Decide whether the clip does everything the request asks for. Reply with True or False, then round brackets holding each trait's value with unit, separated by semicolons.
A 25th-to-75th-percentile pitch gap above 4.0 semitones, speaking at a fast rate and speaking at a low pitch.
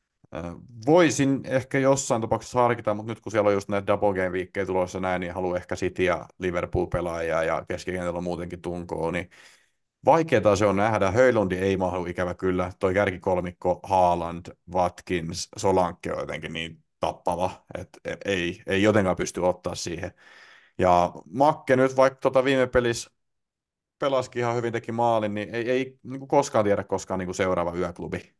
True (4.9 semitones; 160 wpm; 95 Hz)